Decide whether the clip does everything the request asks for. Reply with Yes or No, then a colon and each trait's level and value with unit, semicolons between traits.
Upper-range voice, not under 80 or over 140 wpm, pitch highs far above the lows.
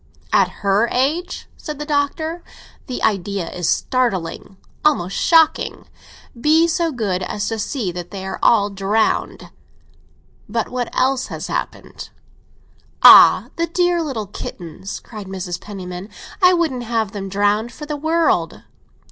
Yes: high, 230 Hz; slow, 135 wpm; wide, 7.5 semitones